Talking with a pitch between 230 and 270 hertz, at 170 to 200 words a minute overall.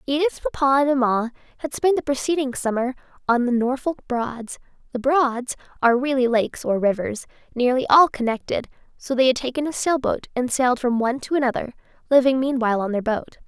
Yes: very high, 260 Hz; average, 180 wpm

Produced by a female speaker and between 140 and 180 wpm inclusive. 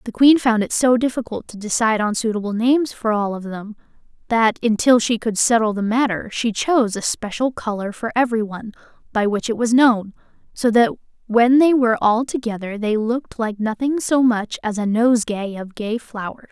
No: female; average, 195 wpm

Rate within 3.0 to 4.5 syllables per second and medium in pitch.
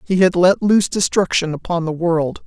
No: 5.2 syllables/s; medium, 175 Hz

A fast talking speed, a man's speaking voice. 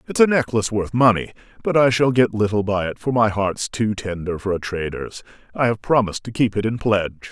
Yes: fast, 230 wpm; male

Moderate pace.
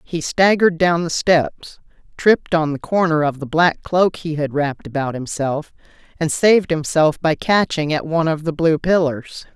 Yes: average, 180 wpm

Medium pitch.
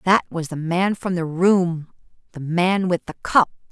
Yes: medium, 175 Hz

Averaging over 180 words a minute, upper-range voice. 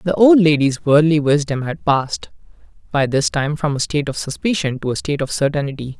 No: average, 200 wpm; medium, 150 Hz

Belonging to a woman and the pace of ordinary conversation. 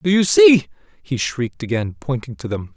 No: male; average, 195 wpm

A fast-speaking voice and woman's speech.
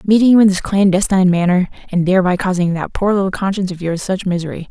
Yes: fast, 215 wpm; female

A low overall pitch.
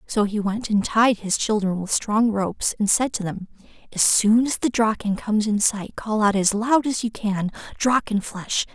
No: high, 215 Hz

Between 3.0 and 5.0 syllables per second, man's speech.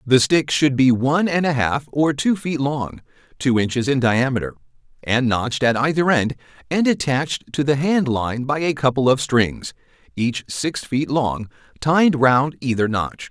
Yes: 4.5 syllables/s; male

